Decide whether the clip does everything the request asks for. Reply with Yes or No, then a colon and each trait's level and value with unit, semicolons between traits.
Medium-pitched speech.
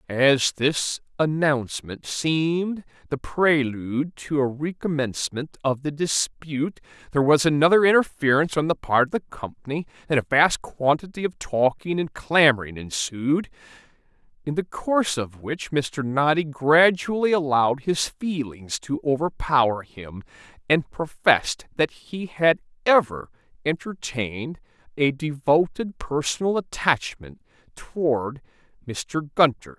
Yes: medium, 145 Hz